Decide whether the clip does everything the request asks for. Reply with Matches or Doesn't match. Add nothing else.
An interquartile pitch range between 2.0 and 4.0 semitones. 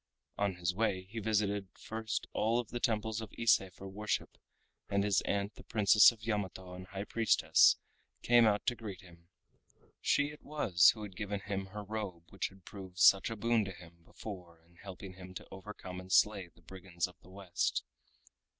Matches